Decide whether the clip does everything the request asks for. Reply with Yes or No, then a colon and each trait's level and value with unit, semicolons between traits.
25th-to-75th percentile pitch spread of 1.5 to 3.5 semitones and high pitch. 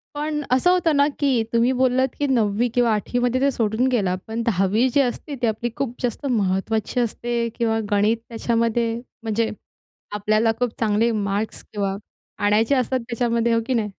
Yes: average, 2.7 semitones; high, 230 Hz